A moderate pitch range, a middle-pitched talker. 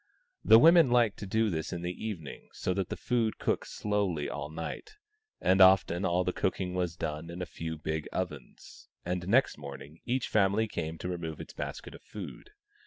No: average, 4.5 semitones; very low, 90 Hz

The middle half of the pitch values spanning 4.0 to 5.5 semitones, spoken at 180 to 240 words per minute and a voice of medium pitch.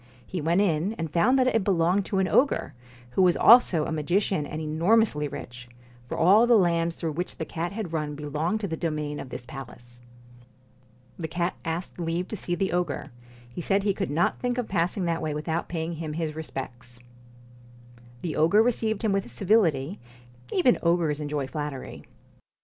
Yes: average, 4.3 semitones; average, 185 wpm; medium, 170 Hz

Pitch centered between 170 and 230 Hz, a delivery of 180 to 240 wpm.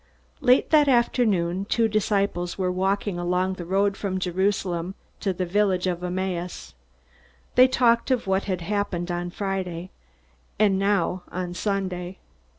No: high, 190 Hz; average, 140 wpm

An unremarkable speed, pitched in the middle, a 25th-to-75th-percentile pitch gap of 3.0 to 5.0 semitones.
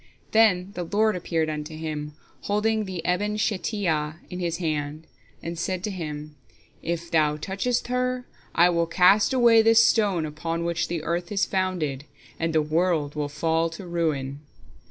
Yes: average, 160 wpm; medium, 170 Hz; average, 4.3 semitones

